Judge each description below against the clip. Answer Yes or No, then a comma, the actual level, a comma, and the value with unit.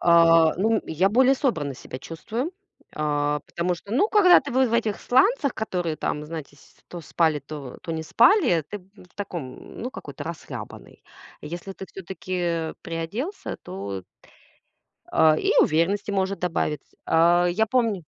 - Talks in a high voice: No, medium, 175 Hz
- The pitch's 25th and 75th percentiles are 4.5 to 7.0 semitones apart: Yes, wide, 5.4 semitones